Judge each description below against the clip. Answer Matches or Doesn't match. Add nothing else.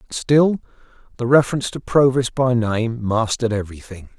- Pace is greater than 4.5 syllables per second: Matches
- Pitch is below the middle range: Matches